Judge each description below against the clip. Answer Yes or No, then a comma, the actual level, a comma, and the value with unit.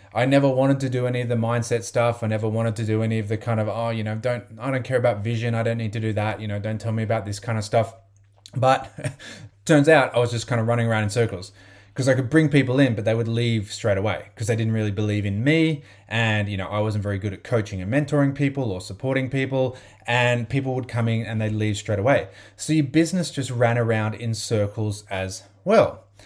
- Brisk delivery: Yes, fast, 255 wpm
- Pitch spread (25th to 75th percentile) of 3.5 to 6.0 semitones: No, average, 3.0 semitones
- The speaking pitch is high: No, low, 115 Hz